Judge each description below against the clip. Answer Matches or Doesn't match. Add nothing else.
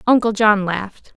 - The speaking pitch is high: Matches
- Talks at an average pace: Matches